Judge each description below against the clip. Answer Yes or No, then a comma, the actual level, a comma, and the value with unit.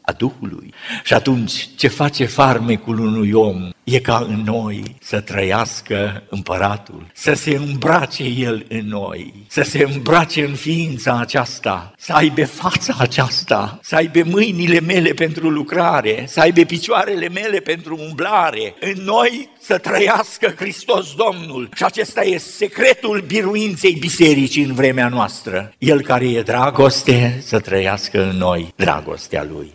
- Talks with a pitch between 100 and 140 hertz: Yes, low, 135 Hz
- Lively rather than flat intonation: Yes, wide, 6.9 semitones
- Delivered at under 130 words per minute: No, average, 140 wpm